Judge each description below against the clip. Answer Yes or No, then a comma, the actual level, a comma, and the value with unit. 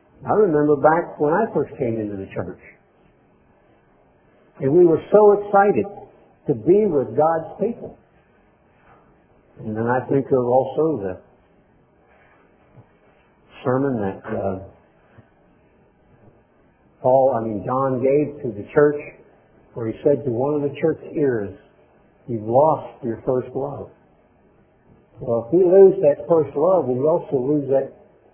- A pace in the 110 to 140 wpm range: Yes, slow, 135 wpm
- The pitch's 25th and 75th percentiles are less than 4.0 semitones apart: No, average, 4.5 semitones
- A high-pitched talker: No, low, 135 Hz